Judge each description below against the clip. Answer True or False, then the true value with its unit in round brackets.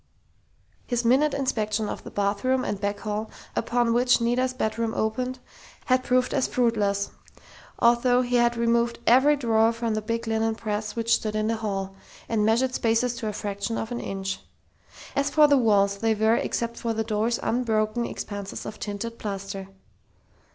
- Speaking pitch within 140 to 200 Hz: False (230 Hz)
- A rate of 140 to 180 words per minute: True (170 wpm)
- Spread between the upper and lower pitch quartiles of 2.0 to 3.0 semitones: True (2.4 semitones)